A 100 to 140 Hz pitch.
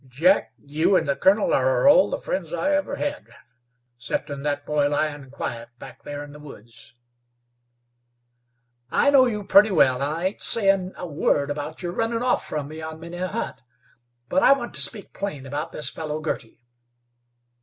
No: medium, 155 Hz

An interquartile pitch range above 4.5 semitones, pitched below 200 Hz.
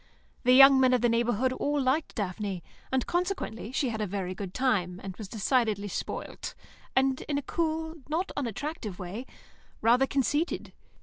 No: wide, 5.4 semitones; very high, 250 Hz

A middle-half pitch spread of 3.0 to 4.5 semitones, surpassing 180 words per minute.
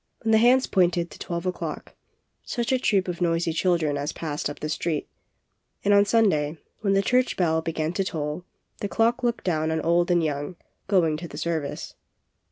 Yes: average, 4.0 semitones; average, 200 wpm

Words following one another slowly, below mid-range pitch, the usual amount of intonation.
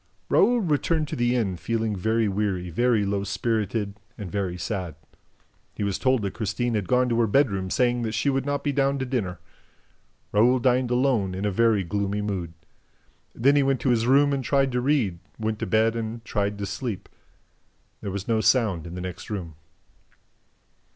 No: average, 190 wpm; low, 110 Hz; average, 4.1 semitones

